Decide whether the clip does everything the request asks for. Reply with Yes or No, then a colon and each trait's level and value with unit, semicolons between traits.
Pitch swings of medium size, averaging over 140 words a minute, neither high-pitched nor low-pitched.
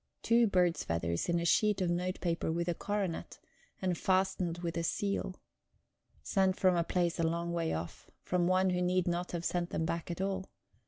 No: narrow, 1.8 semitones; average, 200 wpm; medium, 175 Hz